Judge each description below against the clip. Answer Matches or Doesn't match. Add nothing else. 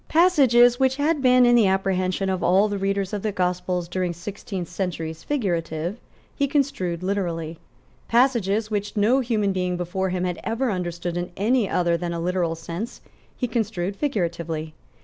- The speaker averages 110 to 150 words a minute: Doesn't match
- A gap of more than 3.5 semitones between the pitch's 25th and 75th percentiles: Matches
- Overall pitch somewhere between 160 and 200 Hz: Matches